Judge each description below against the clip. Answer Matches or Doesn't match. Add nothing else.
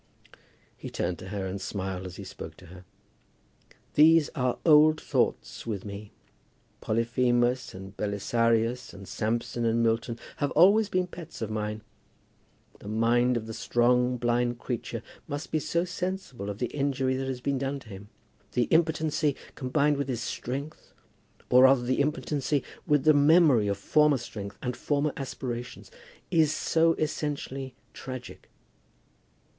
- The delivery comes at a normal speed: Matches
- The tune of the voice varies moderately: Matches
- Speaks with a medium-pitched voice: Doesn't match